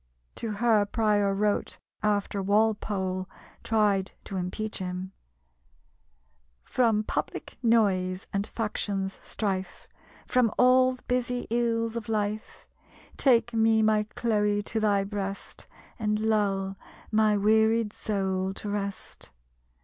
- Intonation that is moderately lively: No, narrow, 2.2 semitones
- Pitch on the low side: No, high, 210 Hz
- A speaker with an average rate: No, slow, 110 wpm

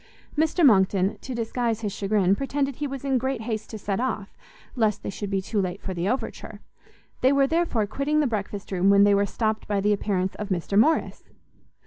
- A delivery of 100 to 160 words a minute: No, fast, 205 wpm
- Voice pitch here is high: Yes, high, 215 Hz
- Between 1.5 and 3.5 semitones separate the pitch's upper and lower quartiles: No, average, 4.8 semitones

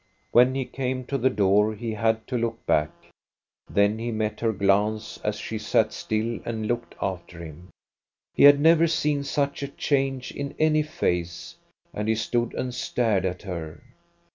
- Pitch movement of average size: Yes, average, 4.1 semitones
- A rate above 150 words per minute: Yes, average, 170 wpm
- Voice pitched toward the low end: Yes, low, 115 Hz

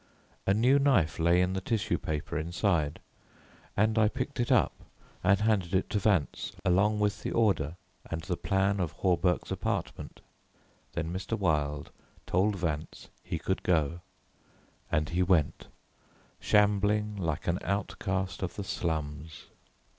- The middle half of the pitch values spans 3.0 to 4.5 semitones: Yes, average, 3.8 semitones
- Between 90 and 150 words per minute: Yes, average, 140 wpm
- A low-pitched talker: Yes, very low, 95 Hz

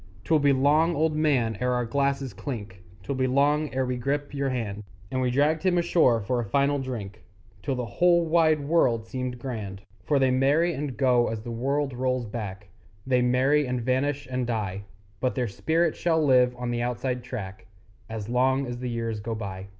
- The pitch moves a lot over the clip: No, average, 3.4 semitones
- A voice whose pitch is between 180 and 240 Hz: No, low, 130 Hz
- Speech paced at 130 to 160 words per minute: No, average, 195 wpm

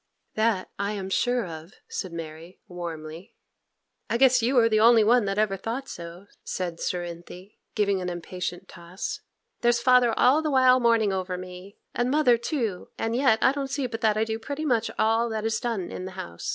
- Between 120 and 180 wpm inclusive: No, average, 195 wpm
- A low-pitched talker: No, high, 215 Hz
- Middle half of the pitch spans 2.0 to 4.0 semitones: No, average, 4.8 semitones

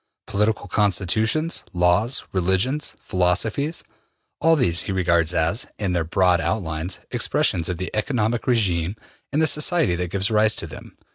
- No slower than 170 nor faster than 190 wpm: No, average, 145 wpm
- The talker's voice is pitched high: No, low, 100 Hz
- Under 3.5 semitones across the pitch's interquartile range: No, average, 4.4 semitones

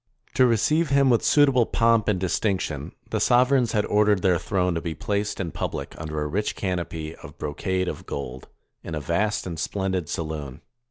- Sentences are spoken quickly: No, average, 180 wpm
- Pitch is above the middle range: No, very low, 95 Hz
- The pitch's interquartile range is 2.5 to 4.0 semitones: No, average, 5.3 semitones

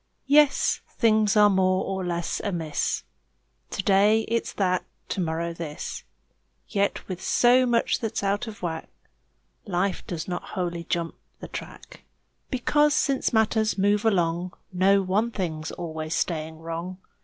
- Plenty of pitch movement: No, average, 4.2 semitones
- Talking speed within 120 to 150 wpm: Yes, average, 140 wpm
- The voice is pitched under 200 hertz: Yes, high, 190 Hz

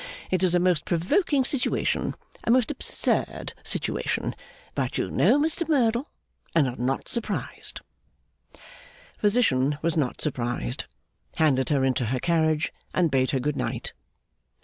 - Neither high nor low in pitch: Yes, medium, 165 Hz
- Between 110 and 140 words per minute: Yes, slow, 135 wpm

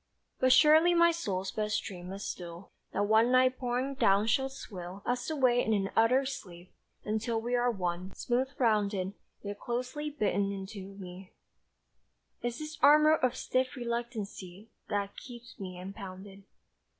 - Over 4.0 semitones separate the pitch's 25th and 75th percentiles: Yes, average, 4.6 semitones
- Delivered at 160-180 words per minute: No, average, 150 wpm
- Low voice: No, high, 220 Hz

